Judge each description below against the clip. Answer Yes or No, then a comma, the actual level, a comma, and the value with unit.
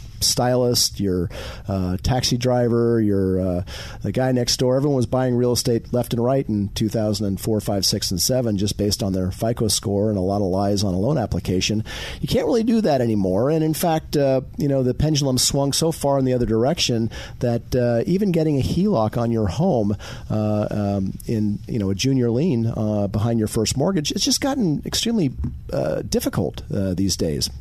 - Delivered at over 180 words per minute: Yes, average, 200 wpm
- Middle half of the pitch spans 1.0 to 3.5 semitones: No, average, 4.3 semitones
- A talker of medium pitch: No, low, 115 Hz